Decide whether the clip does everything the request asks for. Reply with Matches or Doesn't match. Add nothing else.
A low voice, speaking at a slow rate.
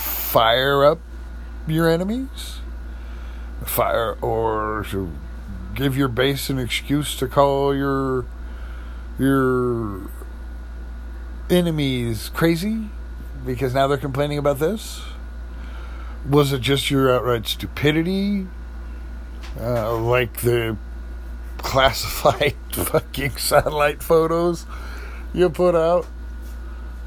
Matches